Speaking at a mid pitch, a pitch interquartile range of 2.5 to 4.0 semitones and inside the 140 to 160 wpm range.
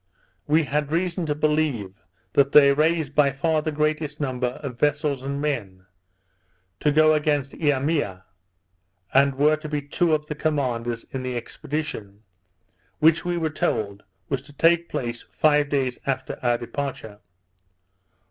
Yes: medium, 145 Hz; average, 3.1 semitones; average, 145 wpm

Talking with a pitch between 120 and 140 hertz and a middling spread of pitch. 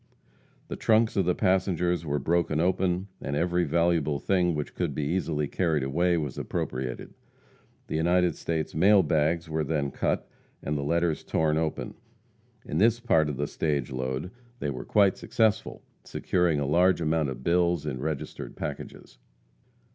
No: very low, 80 Hz; average, 3.2 semitones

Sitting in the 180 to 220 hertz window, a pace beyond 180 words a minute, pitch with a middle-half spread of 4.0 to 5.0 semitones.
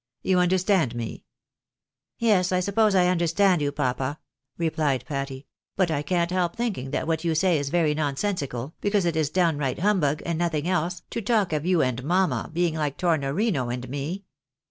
No: medium, 165 Hz; average, 190 wpm; average, 4.3 semitones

